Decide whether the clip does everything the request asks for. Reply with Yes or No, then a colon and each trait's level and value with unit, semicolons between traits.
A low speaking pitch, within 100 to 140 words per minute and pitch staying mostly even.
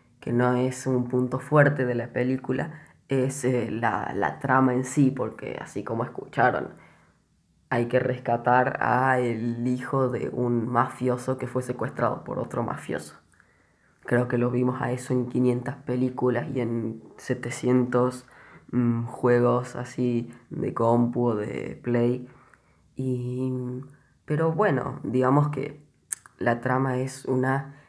Yes: low, 125 Hz; average, 135 wpm; narrow, 1.2 semitones